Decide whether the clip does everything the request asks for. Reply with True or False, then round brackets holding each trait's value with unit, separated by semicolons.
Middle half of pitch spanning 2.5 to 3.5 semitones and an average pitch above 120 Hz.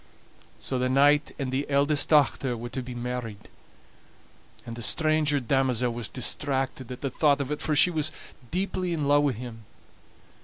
True (2.9 semitones; 135 Hz)